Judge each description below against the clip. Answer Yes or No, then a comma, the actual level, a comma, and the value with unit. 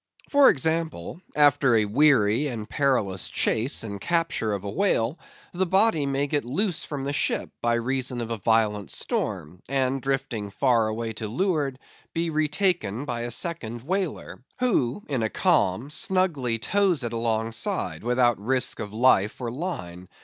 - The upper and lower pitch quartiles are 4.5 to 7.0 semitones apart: Yes, wide, 5.5 semitones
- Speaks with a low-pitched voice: Yes, low, 130 Hz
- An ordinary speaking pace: Yes, average, 155 wpm